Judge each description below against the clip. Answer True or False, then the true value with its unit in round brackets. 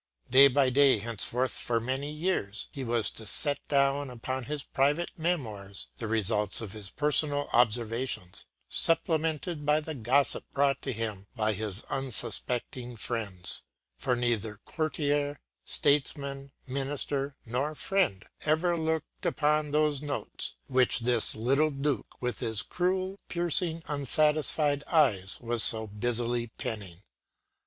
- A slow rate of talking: True (130 wpm)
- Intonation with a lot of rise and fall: False (4.5 semitones)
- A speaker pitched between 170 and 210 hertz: False (135 Hz)